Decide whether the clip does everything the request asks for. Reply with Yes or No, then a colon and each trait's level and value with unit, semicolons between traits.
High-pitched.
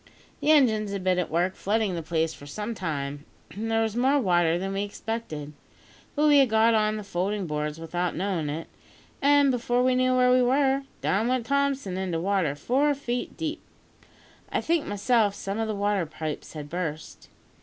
Yes: high, 205 Hz